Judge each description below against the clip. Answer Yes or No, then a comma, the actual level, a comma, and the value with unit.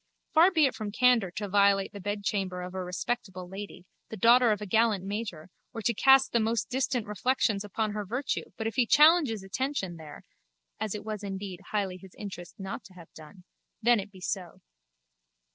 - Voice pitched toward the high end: Yes, high, 205 Hz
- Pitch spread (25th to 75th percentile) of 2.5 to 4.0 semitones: Yes, average, 3.7 semitones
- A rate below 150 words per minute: No, average, 195 wpm